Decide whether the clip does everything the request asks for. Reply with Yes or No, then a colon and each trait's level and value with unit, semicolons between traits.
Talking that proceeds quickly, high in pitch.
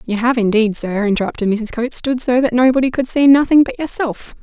Yes: fast, 215 wpm; high, 240 Hz